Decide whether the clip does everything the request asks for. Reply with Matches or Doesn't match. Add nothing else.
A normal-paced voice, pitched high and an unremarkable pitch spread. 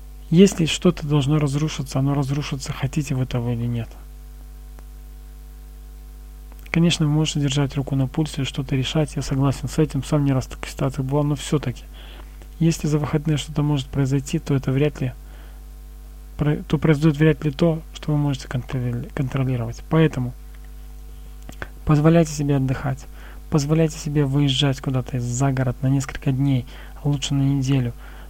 Doesn't match